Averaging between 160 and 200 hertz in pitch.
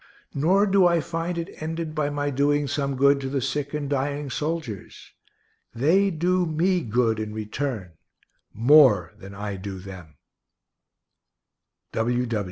No: medium, 145 Hz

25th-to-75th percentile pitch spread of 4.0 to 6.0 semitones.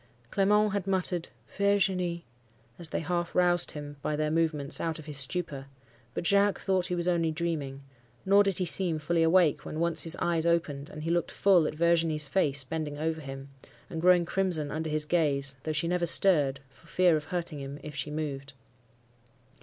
No: average, 3.0 semitones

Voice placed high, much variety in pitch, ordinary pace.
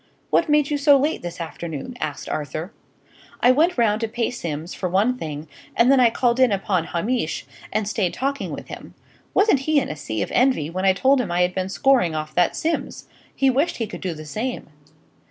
No: high, 215 Hz; wide, 7.5 semitones; fast, 215 wpm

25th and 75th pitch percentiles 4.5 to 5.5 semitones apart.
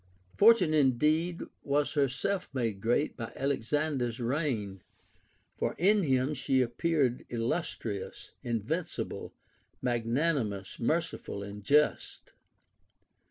Yes: average, 5.0 semitones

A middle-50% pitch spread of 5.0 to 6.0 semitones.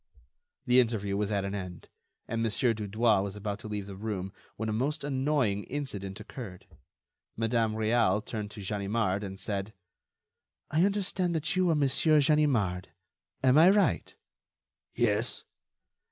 Yes: wide, 5.4 semitones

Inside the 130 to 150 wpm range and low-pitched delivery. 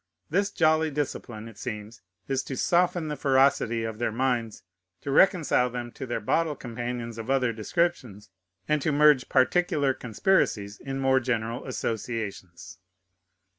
Yes: average, 140 wpm; low, 125 Hz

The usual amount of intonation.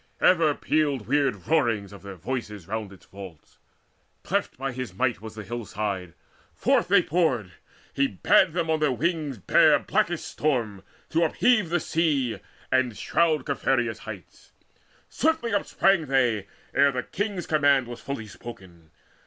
No: wide, 6.8 semitones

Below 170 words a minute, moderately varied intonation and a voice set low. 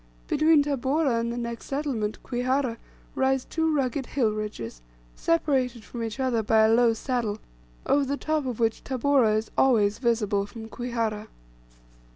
No: average, 155 wpm; average, 3.5 semitones; high, 240 Hz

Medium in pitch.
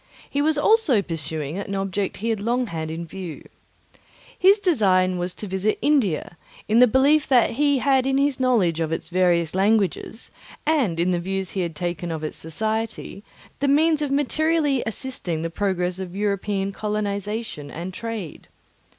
No: high, 200 Hz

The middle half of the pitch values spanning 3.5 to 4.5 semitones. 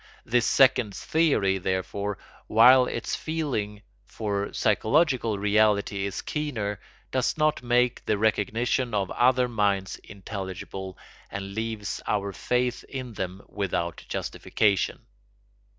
Yes: average, 3.8 semitones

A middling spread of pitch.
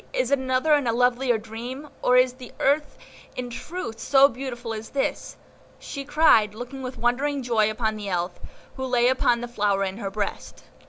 Yes: average, 3.3 semitones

